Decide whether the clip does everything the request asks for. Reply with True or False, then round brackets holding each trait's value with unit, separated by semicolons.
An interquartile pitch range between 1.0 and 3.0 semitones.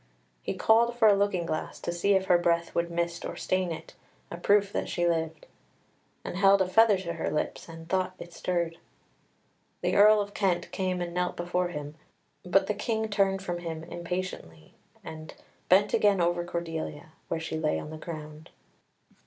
True (2.7 semitones)